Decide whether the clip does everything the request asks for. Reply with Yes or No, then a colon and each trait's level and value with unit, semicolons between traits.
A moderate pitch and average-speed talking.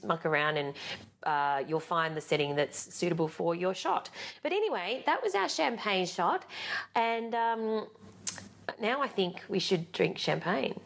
Yes: medium, 180 Hz; average, 160 wpm